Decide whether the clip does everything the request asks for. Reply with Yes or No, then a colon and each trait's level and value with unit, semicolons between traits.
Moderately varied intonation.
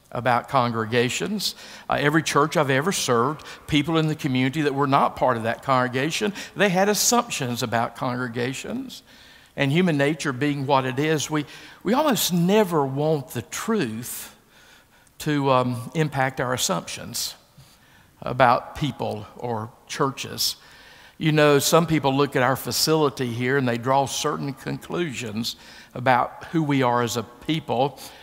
Yes: average, 4.1 semitones